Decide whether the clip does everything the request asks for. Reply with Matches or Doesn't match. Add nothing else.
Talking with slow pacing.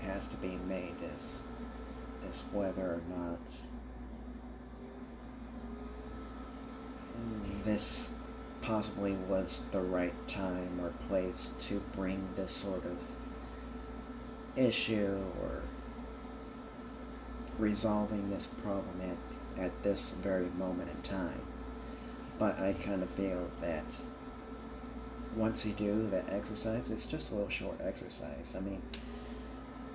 Matches